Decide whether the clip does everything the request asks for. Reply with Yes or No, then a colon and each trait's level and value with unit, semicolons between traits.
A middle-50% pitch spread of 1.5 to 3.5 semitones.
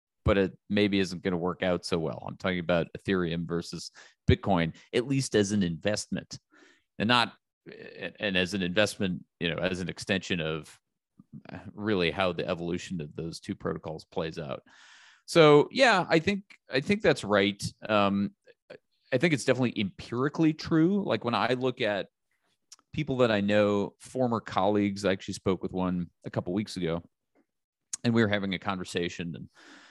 No: average, 5.1 semitones